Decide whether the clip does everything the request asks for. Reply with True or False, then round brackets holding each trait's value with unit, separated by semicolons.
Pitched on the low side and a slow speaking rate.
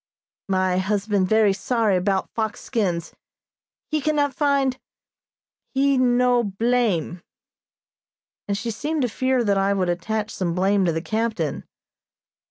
False (215 Hz; 130 wpm)